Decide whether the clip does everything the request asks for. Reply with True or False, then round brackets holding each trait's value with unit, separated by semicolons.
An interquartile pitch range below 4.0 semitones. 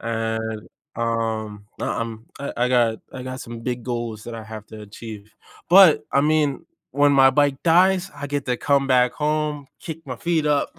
False (4.4 semitones)